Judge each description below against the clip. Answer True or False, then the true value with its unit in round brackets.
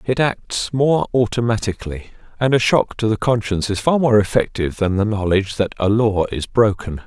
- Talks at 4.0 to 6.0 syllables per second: True (5.4 syllables/s)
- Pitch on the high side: False (110 Hz)